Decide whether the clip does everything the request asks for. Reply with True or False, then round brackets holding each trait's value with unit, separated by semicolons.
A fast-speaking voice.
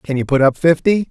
True (270 wpm)